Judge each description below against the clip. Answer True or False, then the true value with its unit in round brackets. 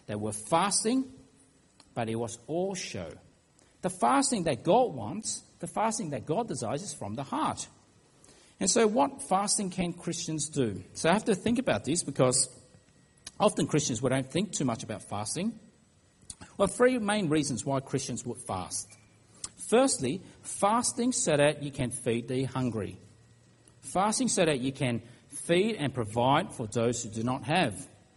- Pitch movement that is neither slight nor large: False (8.3 semitones)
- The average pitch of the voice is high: False (140 Hz)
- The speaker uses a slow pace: False (165 wpm)